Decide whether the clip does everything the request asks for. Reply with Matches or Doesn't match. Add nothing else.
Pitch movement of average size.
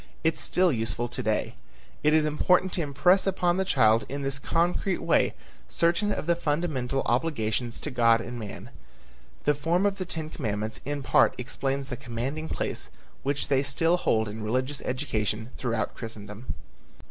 Doesn't match